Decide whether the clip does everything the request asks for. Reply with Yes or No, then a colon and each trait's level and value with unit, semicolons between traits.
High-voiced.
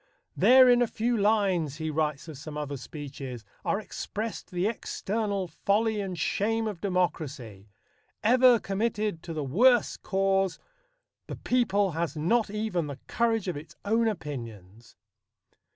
Yes: high, 195 Hz